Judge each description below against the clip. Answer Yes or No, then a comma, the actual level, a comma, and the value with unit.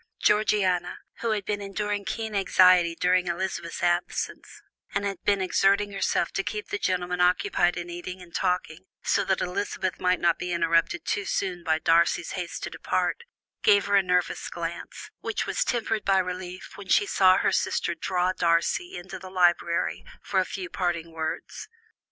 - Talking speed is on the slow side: No, average, 170 wpm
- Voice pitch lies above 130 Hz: Yes, medium, 185 Hz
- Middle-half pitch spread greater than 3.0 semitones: No, narrow, 2.4 semitones